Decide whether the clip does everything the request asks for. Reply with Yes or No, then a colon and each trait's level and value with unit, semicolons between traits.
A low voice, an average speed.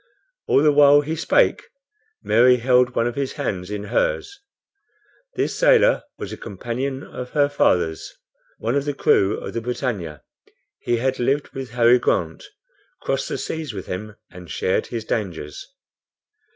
Yes: low, 125 Hz; average, 155 wpm